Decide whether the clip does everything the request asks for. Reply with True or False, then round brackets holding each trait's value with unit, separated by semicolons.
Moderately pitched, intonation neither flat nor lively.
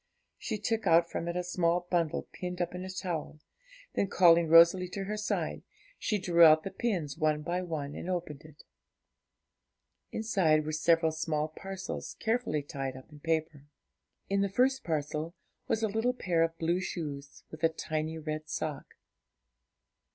True (170 Hz; 3.2 semitones)